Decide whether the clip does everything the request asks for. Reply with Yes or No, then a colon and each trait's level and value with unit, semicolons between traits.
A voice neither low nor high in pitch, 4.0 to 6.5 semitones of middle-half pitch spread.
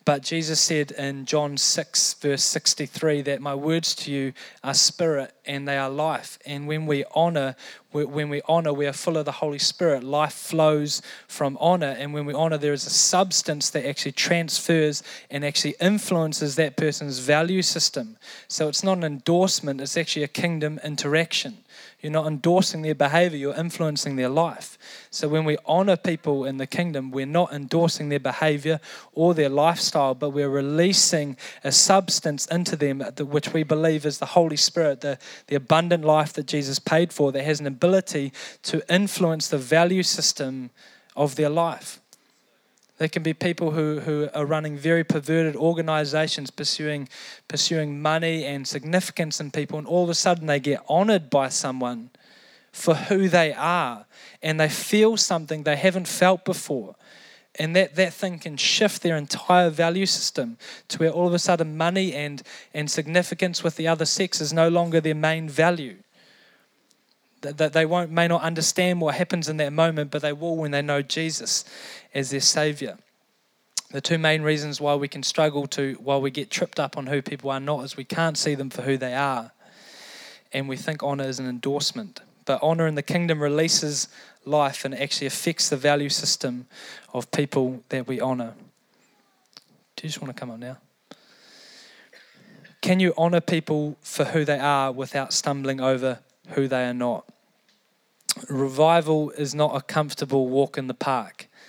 No: medium, 155 Hz; average, 2.9 semitones